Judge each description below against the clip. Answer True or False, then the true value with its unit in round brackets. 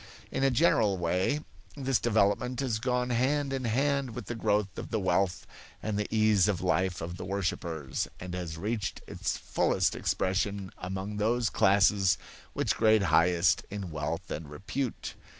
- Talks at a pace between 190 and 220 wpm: False (160 wpm)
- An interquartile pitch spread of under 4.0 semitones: False (4.6 semitones)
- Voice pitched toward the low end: True (100 Hz)